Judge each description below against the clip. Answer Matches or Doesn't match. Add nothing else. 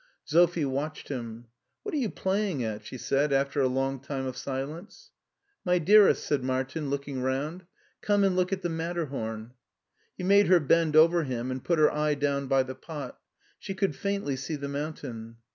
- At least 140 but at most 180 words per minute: Doesn't match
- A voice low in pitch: Doesn't match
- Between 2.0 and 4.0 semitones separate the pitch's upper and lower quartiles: Doesn't match